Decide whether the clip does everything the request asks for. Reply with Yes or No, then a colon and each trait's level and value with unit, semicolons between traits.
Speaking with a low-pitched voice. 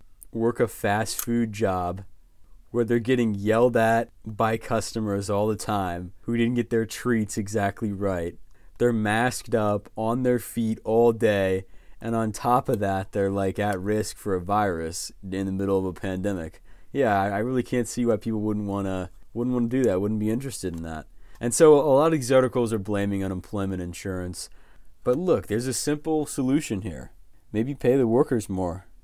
Yes: low, 110 Hz